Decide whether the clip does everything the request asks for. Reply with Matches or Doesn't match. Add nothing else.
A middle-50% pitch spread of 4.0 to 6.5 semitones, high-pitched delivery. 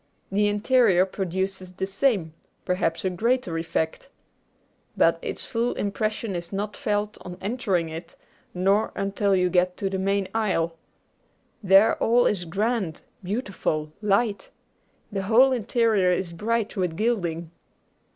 Doesn't match